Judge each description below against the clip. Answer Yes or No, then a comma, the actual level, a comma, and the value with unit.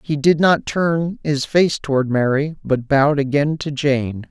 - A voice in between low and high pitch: Yes, medium, 145 Hz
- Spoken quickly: No, average, 180 wpm